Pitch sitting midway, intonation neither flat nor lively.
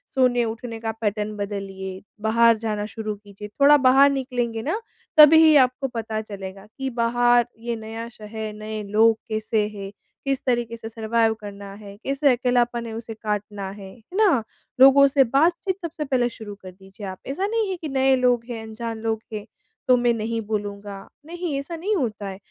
No: high, 230 Hz; average, 3.8 semitones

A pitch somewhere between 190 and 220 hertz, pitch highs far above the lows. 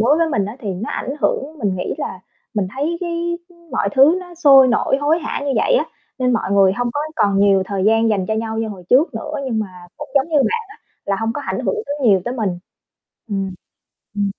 No: high, 240 Hz; wide, 6.5 semitones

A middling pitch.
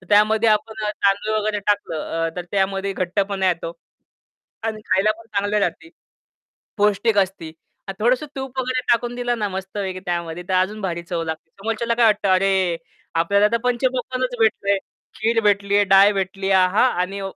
No: high, 200 Hz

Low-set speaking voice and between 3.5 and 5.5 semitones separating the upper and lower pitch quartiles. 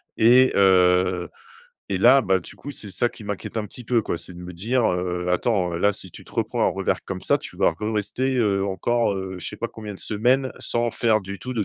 Yes: low, 105 Hz; average, 4.3 semitones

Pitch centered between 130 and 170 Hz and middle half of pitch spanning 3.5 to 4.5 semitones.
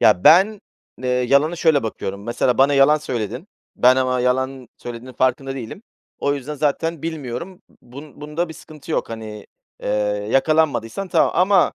Yes: low, 135 Hz; average, 4.2 semitones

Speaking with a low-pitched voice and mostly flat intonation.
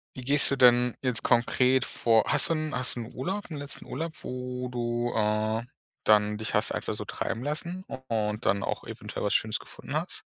No: low, 125 Hz; average, 3.5 semitones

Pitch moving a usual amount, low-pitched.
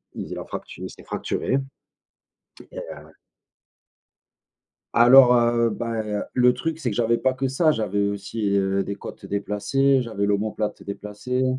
Yes: average, 3.7 semitones; low, 115 Hz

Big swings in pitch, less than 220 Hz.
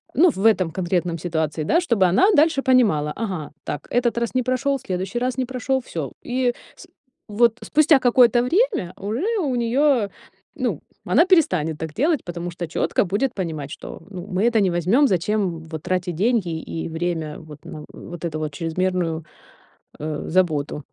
Yes: wide, 7.4 semitones; high, 190 Hz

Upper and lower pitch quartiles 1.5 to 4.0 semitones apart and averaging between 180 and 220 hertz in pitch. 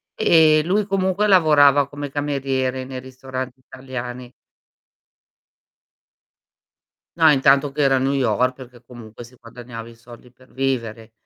No: narrow, 2.6 semitones; low, 130 Hz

